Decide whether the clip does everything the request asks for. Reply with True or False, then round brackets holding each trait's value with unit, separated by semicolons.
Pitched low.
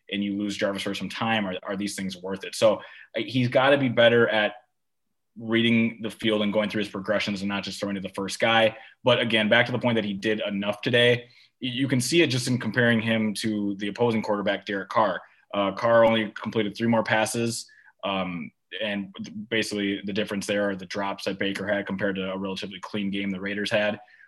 True (105 Hz)